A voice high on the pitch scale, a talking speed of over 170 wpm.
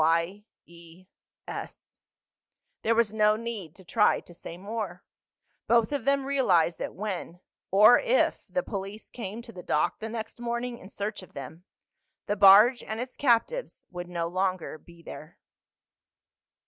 No: high, 205 Hz; average, 145 wpm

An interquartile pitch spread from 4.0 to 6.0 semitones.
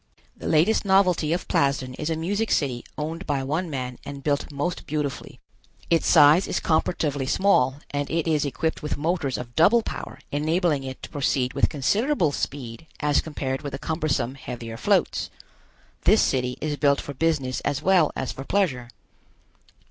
No: average, 3.5 semitones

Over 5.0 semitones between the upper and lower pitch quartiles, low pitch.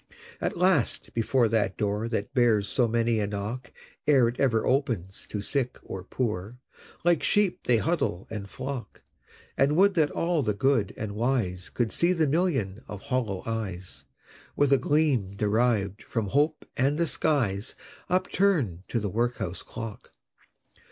Yes: wide, 5.5 semitones; low, 120 Hz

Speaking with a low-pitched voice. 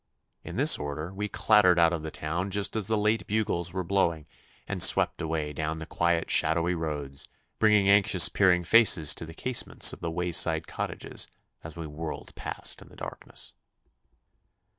Yes: very low, 85 Hz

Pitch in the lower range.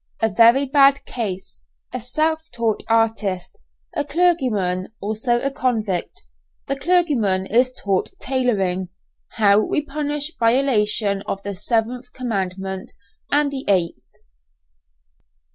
No: high, 230 Hz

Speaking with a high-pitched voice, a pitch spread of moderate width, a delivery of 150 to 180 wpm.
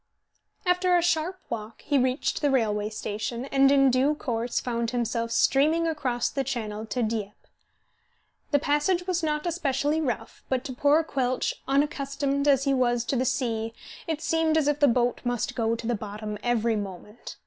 Yes: very high, 260 Hz; average, 4.2 semitones; average, 175 wpm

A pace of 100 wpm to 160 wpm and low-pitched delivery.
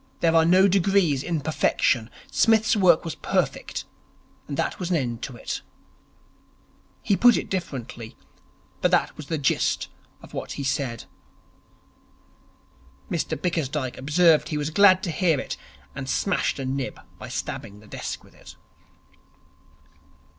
No: average, 145 wpm; medium, 155 Hz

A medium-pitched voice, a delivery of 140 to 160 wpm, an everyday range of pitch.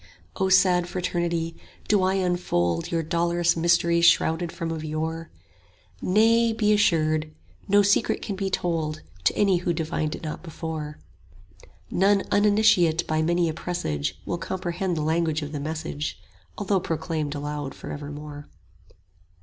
Yes: medium, 170 Hz; average, 150 wpm; average, 3.1 semitones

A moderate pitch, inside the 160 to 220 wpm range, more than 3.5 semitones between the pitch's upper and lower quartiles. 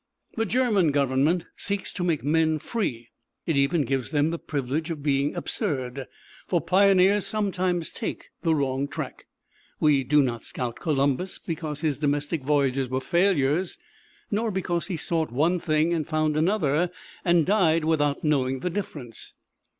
No: medium, 155 Hz; average, 150 wpm; average, 4.1 semitones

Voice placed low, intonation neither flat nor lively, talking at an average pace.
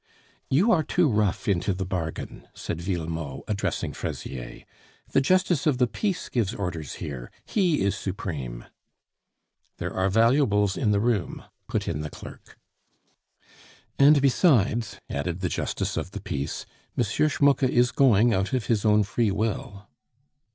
No: low, 105 Hz; wide, 6.2 semitones; average, 145 wpm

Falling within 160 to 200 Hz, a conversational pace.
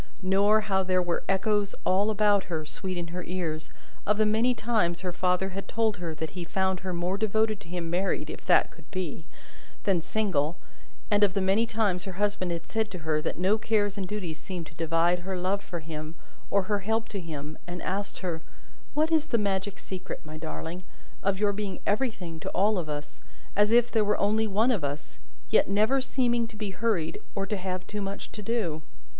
No: high, 190 Hz; fast, 210 wpm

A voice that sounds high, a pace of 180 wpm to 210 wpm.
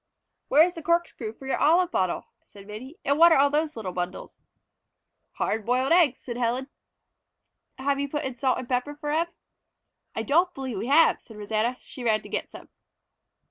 Yes: very high, 265 Hz; average, 190 wpm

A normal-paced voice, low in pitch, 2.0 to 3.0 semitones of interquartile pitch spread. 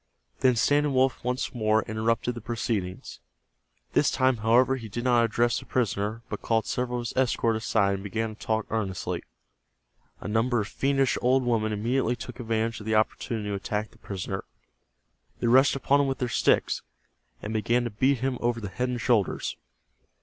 Yes: average, 185 wpm; low, 115 Hz; narrow, 2.5 semitones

